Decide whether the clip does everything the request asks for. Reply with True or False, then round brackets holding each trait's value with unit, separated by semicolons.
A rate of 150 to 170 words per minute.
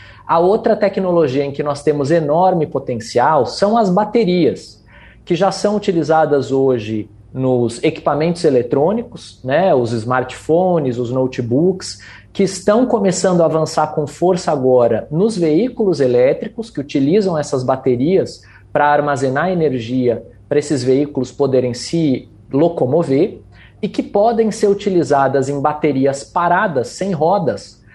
False (125 wpm)